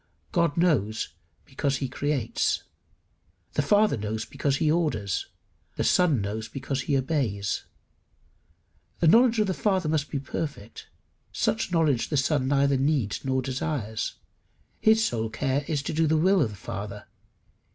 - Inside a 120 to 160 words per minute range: Yes, average, 150 wpm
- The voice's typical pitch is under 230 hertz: Yes, medium, 140 Hz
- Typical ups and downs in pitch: No, wide, 5.7 semitones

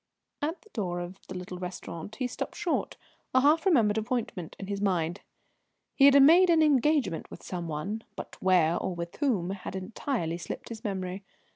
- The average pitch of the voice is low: No, high, 200 Hz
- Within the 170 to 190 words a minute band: Yes, average, 180 wpm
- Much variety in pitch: Yes, wide, 7.1 semitones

